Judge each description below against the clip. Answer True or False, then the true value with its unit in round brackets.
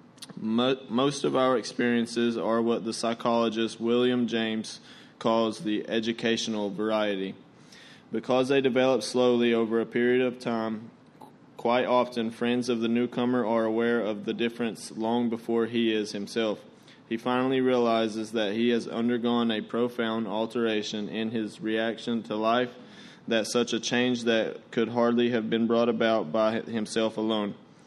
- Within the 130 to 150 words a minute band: True (145 wpm)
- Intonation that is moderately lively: False (1.4 semitones)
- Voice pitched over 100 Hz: True (115 Hz)